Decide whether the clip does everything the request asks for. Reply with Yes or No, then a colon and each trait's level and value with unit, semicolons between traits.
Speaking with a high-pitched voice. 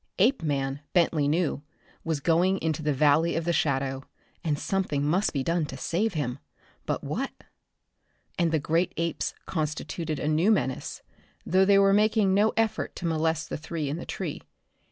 No: medium, 165 Hz